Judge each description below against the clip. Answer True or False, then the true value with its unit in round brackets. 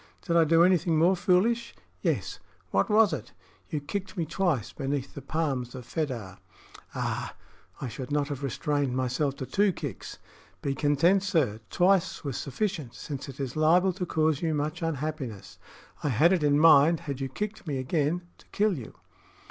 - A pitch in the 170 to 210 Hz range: False (155 Hz)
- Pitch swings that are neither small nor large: True (4.4 semitones)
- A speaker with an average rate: True (175 wpm)